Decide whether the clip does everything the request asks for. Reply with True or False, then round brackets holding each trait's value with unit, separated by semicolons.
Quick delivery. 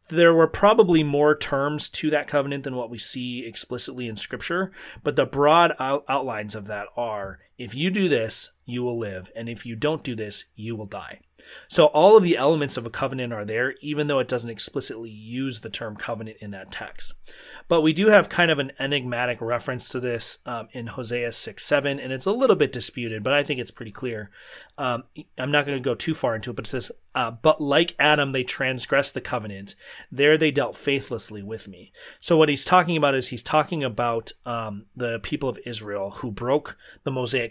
True (215 wpm)